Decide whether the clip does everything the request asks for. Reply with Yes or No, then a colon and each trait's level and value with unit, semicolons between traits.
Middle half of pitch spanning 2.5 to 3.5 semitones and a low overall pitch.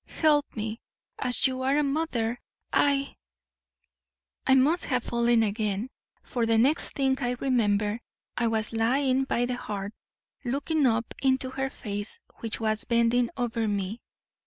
No: average, 3.2 semitones; high, 240 Hz